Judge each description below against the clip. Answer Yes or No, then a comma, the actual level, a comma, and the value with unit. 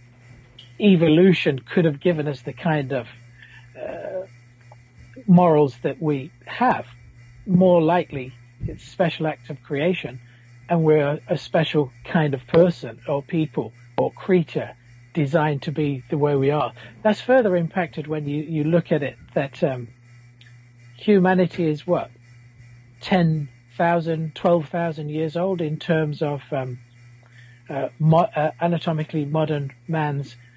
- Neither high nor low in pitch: Yes, medium, 150 Hz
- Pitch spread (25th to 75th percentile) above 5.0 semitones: Yes, wide, 5.4 semitones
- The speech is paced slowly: Yes, slow, 130 wpm